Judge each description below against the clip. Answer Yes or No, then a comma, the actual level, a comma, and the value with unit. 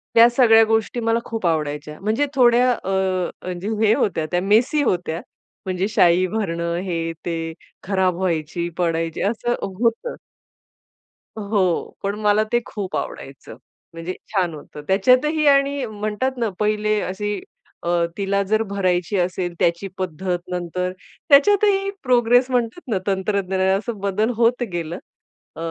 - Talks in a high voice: Yes, high, 200 Hz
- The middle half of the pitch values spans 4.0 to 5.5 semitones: Yes, average, 4.6 semitones